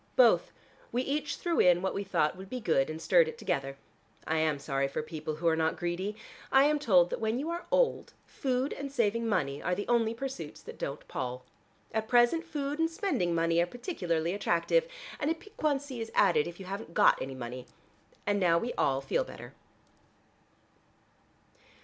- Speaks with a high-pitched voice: Yes, high, 195 Hz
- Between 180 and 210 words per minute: Yes, average, 190 wpm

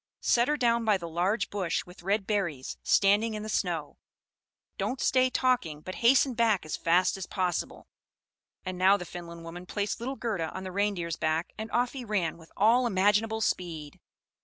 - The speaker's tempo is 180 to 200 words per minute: Yes, average, 185 wpm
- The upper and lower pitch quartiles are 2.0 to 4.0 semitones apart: No, average, 4.6 semitones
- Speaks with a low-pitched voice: No, high, 195 Hz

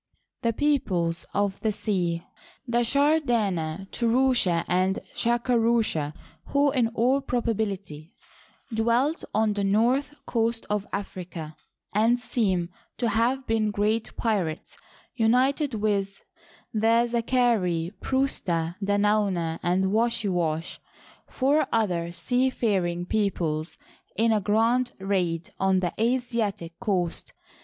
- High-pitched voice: Yes, high, 215 Hz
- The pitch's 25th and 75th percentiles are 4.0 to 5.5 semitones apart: Yes, average, 4.7 semitones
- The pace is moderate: No, slow, 115 wpm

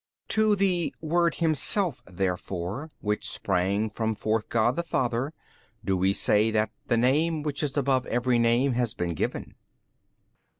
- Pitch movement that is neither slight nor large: No, wide, 6.4 semitones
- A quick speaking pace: No, average, 155 wpm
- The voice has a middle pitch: No, low, 120 Hz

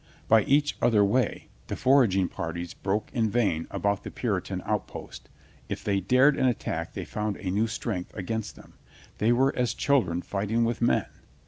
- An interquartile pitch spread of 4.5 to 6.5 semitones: No, average, 3.8 semitones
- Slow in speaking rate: No, average, 185 wpm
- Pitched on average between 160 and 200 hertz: No, low, 110 Hz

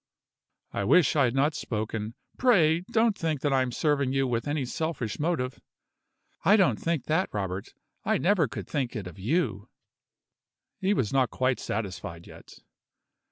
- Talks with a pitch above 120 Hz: Yes, low, 135 Hz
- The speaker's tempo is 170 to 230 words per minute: No, average, 160 wpm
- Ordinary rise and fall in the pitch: No, wide, 6.3 semitones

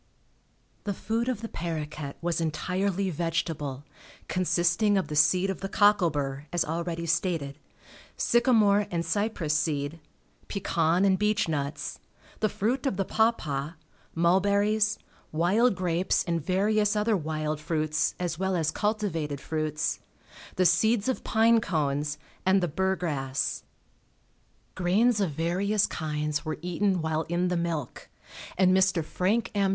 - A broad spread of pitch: No, average, 4.4 semitones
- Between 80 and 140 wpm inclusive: Yes, slow, 135 wpm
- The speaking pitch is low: No, medium, 175 Hz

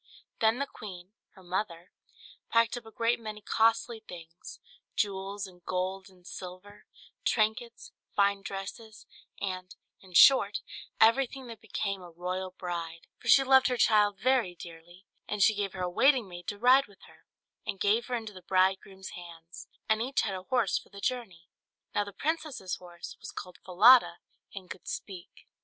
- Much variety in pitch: No, average, 3.8 semitones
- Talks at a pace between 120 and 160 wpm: No, average, 170 wpm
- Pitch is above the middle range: Yes, high, 200 Hz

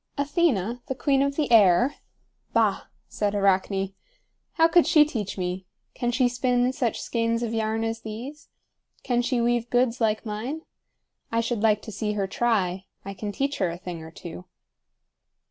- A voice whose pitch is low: No, high, 230 Hz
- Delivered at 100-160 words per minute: No, average, 170 wpm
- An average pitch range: Yes, average, 4.0 semitones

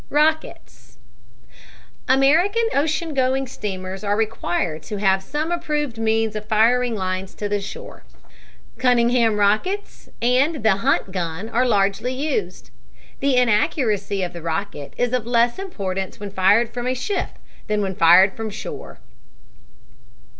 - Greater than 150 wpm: No, slow, 135 wpm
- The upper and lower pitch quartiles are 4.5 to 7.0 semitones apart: Yes, average, 4.8 semitones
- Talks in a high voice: Yes, high, 225 Hz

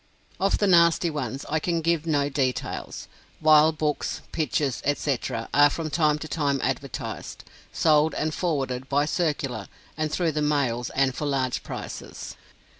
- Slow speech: No, average, 150 wpm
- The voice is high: No, medium, 150 Hz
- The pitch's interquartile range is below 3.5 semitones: Yes, narrow, 2.5 semitones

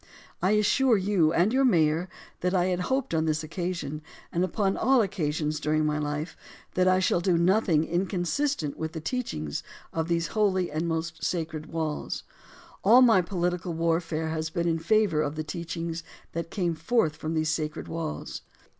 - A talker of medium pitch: Yes, medium, 170 Hz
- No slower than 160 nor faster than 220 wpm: Yes, average, 170 wpm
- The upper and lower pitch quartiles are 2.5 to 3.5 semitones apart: Yes, average, 3.0 semitones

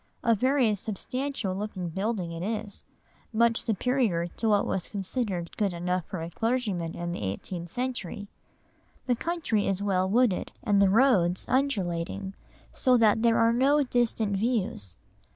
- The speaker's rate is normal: Yes, average, 150 wpm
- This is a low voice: No, high, 205 Hz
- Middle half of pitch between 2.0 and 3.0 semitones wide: No, average, 4.7 semitones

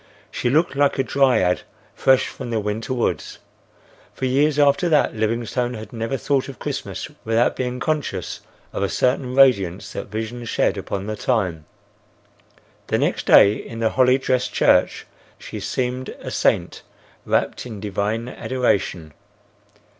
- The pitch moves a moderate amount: Yes, average, 3.5 semitones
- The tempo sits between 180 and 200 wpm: No, average, 145 wpm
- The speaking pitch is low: Yes, low, 120 Hz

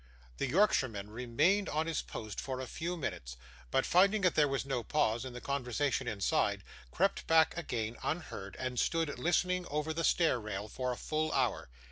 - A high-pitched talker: No, low, 135 Hz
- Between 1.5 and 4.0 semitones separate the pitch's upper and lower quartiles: No, average, 5.3 semitones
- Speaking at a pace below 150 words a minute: No, average, 180 wpm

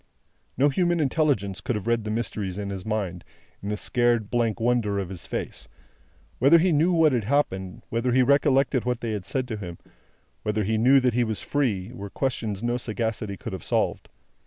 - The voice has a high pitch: No, low, 115 Hz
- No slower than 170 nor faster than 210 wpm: Yes, fast, 205 wpm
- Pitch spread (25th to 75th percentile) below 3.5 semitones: No, average, 4.2 semitones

